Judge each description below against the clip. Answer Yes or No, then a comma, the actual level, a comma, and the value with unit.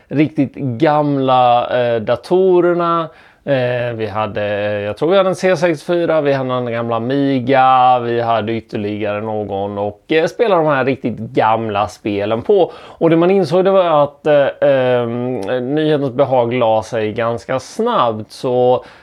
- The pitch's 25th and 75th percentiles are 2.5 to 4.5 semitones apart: No, average, 4.9 semitones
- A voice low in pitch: Yes, low, 125 Hz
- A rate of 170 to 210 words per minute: No, average, 150 wpm